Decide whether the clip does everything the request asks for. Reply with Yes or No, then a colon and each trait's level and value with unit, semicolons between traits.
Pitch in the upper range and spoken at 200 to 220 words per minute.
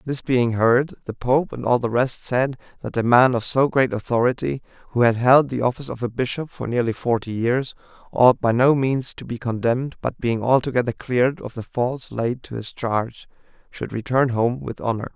No: low, 125 Hz; fast, 205 wpm